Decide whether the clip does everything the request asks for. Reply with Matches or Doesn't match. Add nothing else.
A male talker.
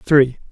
Matches